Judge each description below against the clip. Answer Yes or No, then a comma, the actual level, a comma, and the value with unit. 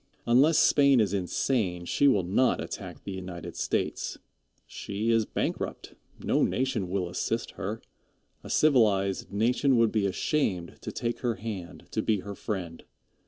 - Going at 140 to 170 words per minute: Yes, average, 150 wpm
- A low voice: Yes, low, 105 Hz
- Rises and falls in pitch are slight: No, average, 4.3 semitones